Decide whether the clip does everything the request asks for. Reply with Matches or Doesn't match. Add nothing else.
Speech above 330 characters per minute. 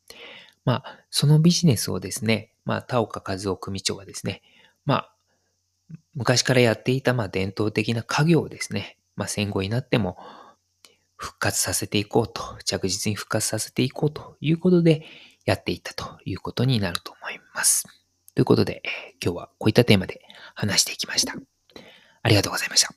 Matches